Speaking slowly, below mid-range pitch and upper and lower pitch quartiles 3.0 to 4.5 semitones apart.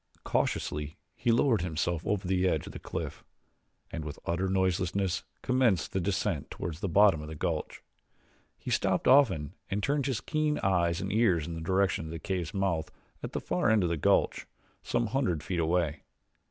No: average, 185 wpm; very low, 90 Hz; average, 4.0 semitones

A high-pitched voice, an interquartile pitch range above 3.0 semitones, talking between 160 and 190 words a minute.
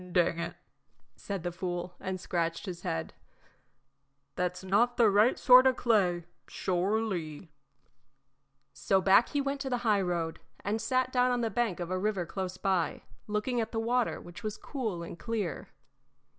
Yes: high, 195 Hz; average, 4.9 semitones; average, 165 wpm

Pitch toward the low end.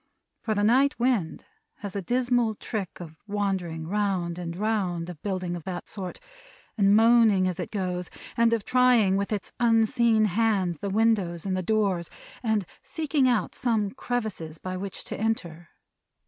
No: high, 205 Hz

